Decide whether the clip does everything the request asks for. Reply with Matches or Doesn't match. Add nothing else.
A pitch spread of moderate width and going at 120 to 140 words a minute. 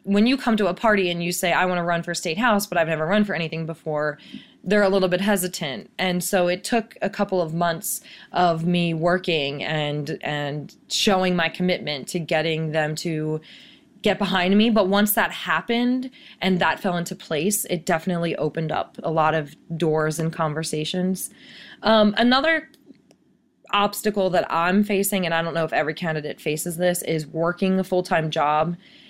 Doesn't match